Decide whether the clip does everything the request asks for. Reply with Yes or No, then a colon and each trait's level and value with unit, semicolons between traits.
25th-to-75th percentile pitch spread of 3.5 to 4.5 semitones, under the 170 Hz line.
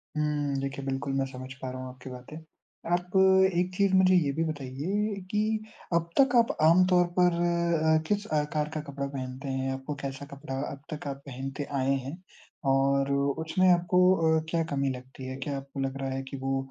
Yes: average, 4.0 semitones; medium, 140 Hz